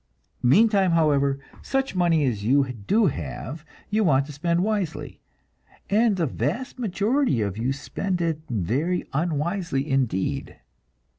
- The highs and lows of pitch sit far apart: Yes, wide, 6.6 semitones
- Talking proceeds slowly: Yes, slow, 130 wpm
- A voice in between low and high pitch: Yes, medium, 160 Hz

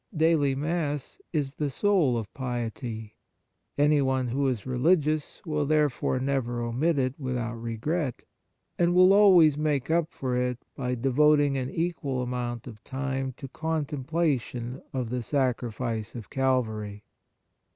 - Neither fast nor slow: No, slow, 130 wpm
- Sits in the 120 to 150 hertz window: Yes, low, 135 Hz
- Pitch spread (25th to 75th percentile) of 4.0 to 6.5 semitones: No, average, 3.6 semitones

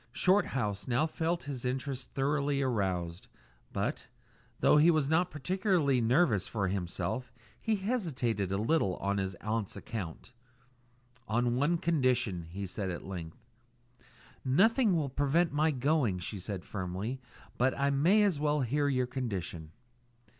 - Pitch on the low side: Yes, low, 130 Hz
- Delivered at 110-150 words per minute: Yes, average, 140 wpm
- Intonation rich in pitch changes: Yes, wide, 7.3 semitones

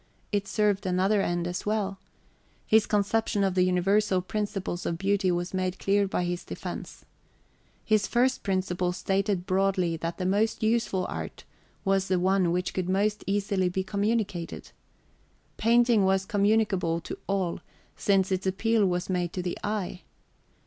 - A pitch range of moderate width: No, narrow, 2.2 semitones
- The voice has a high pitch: Yes, high, 195 Hz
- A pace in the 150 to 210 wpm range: Yes, average, 155 wpm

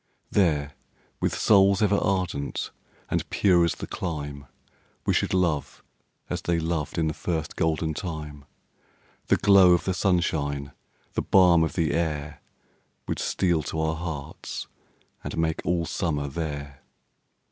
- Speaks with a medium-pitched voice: No, very low, 80 Hz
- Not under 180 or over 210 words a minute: No, average, 140 wpm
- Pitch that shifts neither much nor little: Yes, average, 3.2 semitones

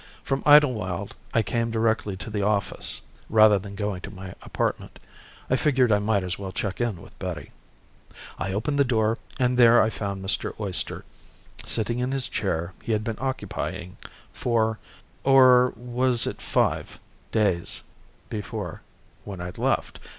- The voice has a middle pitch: No, low, 110 Hz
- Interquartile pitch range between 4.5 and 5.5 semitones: No, average, 3.7 semitones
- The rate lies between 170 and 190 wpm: No, average, 155 wpm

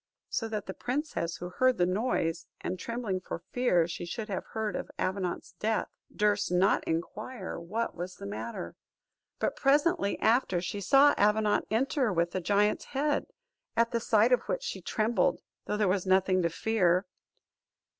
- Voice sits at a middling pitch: No, high, 210 Hz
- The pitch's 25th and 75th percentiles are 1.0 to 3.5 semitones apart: No, average, 4.5 semitones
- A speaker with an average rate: Yes, average, 165 wpm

